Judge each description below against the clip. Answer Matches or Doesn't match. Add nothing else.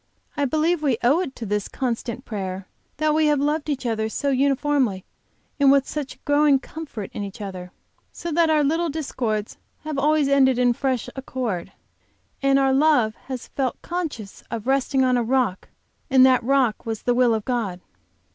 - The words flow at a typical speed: Matches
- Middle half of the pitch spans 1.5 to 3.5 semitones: Doesn't match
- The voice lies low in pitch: Doesn't match